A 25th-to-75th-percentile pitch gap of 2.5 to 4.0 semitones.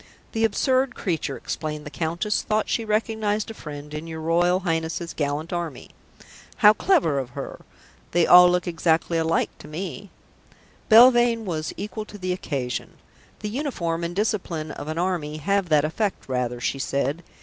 No: average, 5.3 semitones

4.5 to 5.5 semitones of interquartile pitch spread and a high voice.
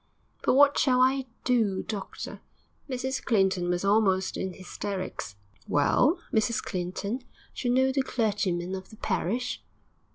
Yes: average, 5.2 semitones; high, 215 Hz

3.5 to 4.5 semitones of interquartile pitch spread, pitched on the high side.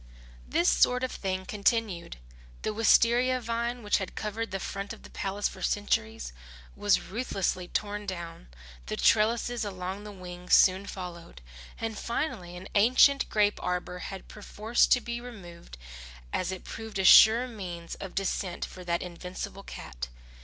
Yes: average, 3.8 semitones; high, 200 Hz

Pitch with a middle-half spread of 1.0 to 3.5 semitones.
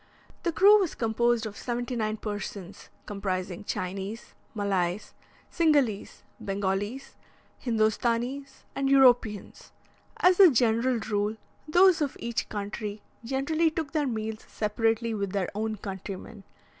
No: average, 4.6 semitones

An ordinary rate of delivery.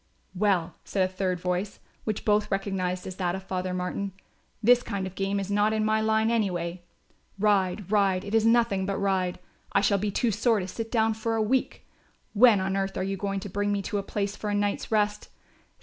No: fast, 215 wpm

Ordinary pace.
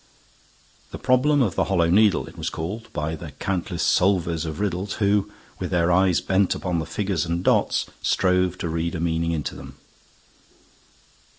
Yes: average, 170 wpm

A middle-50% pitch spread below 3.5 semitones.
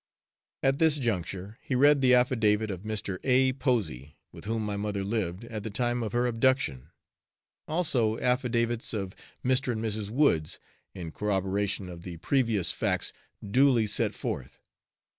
No: average, 4.1 semitones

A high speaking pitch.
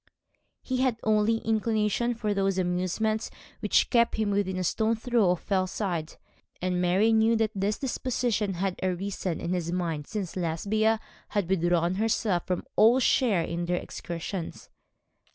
Yes: high, 200 Hz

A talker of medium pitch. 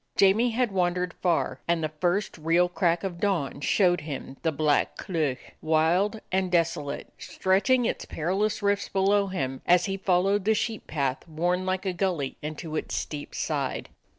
Yes: medium, 180 Hz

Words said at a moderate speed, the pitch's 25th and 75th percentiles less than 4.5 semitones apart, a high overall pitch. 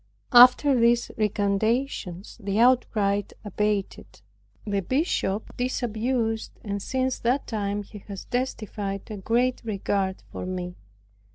No: slow, 110 wpm; average, 3.6 semitones; high, 215 Hz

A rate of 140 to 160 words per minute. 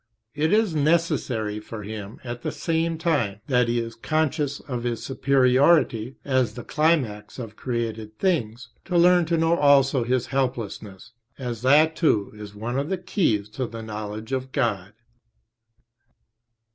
Yes: average, 150 wpm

